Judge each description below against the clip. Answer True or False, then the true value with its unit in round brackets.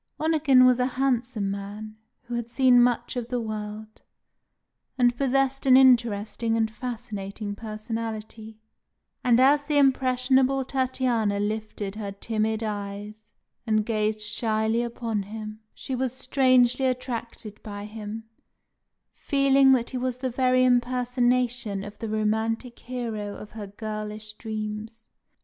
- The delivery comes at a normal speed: False (125 wpm)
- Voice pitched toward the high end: True (230 Hz)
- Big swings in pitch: False (2.9 semitones)